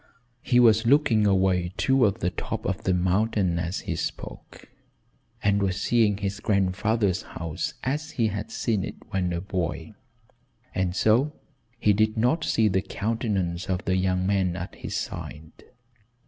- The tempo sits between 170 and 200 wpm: No, average, 155 wpm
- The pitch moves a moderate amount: Yes, average, 3.3 semitones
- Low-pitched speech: Yes, low, 100 Hz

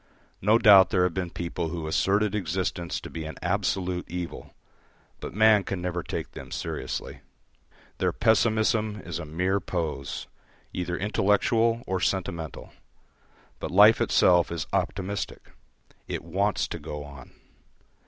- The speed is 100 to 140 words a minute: Yes, slow, 135 wpm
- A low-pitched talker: Yes, very low, 90 Hz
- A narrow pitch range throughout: No, average, 3.3 semitones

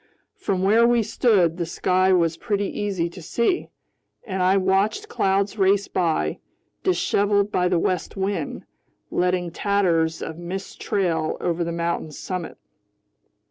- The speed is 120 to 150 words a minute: Yes, average, 140 wpm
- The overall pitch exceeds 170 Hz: Yes, medium, 185 Hz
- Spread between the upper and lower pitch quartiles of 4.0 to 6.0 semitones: No, average, 2.9 semitones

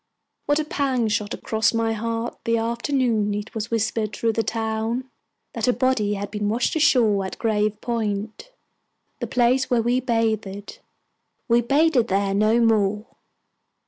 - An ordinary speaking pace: Yes, average, 150 wpm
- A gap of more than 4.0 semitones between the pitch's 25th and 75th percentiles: No, narrow, 2.4 semitones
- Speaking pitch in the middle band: No, high, 225 Hz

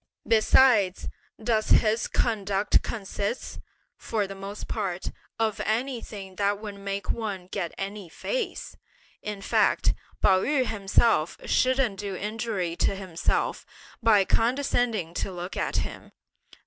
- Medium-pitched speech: No, high, 205 Hz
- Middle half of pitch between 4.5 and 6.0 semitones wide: No, average, 2.7 semitones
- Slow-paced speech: Yes, slow, 120 wpm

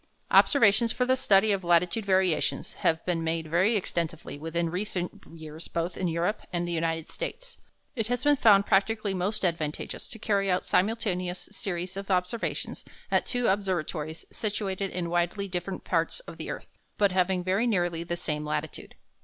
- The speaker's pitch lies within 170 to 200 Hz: Yes, medium, 185 Hz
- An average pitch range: Yes, average, 3.3 semitones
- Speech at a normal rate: Yes, average, 170 wpm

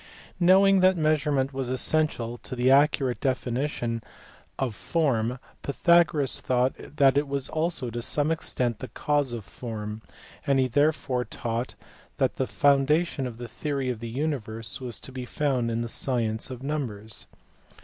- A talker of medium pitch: No, low, 130 Hz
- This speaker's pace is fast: No, average, 155 wpm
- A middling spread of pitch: Yes, average, 3.8 semitones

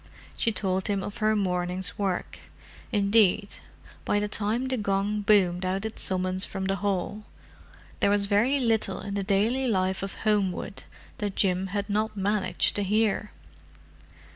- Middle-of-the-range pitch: No, high, 200 Hz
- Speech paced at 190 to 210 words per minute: No, average, 150 wpm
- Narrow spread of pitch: Yes, narrow, 1.9 semitones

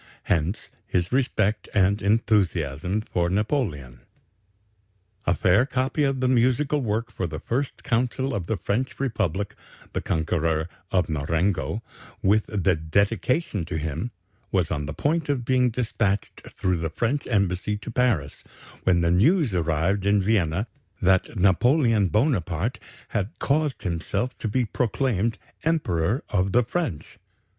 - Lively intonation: Yes, wide, 6.1 semitones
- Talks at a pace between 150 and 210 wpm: No, slow, 135 wpm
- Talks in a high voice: No, low, 105 Hz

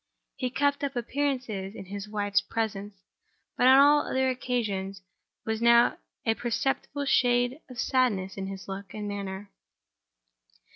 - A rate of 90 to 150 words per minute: Yes, average, 140 wpm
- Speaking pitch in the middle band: No, high, 225 Hz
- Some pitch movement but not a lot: Yes, average, 4.5 semitones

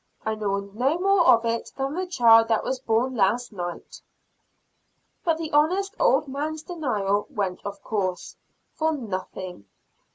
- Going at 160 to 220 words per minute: No, average, 150 wpm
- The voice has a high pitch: Yes, high, 235 Hz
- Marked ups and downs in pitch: Yes, wide, 7.5 semitones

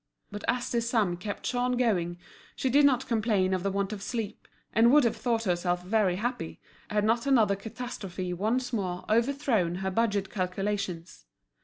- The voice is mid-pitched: No, high, 210 Hz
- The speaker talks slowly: No, average, 170 wpm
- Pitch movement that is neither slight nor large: Yes, average, 4.3 semitones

